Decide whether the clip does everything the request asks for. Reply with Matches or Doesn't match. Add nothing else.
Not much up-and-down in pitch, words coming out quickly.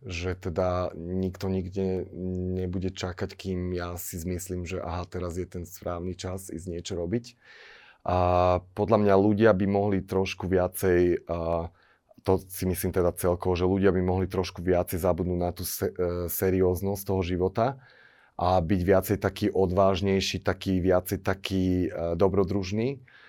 Doesn't match